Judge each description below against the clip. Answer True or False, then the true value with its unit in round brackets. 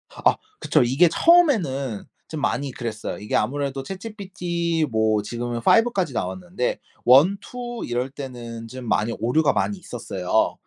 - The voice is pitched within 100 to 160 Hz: True (135 Hz)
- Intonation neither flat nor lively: False (7.5 semitones)